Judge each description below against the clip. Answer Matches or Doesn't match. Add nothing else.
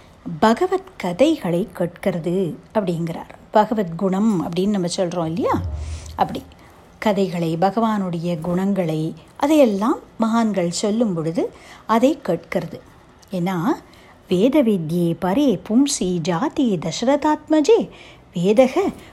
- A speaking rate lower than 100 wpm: Matches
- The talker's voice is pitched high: Matches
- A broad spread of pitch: Matches